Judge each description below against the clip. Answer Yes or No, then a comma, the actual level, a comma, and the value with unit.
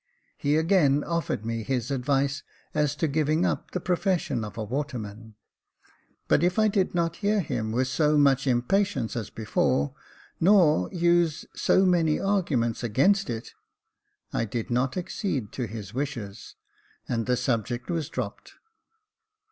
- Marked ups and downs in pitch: Yes, wide, 6.6 semitones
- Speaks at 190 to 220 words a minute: No, average, 150 wpm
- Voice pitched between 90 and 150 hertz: Yes, medium, 140 Hz